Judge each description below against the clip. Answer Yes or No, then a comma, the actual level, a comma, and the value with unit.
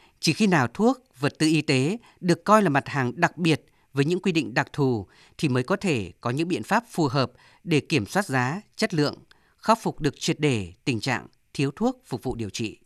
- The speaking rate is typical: Yes, average, 235 wpm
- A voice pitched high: No, medium, 150 Hz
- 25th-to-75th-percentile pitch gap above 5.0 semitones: Yes, wide, 5.4 semitones